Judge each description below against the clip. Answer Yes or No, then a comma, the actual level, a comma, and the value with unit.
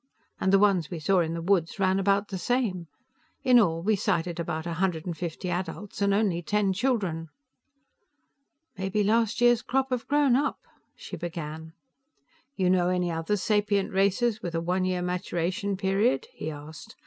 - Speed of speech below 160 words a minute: No, average, 170 wpm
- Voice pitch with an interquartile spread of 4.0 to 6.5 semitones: No, average, 3.4 semitones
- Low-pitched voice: No, high, 190 Hz